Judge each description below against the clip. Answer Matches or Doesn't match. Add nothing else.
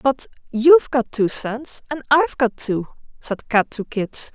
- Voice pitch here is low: Doesn't match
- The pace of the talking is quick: Doesn't match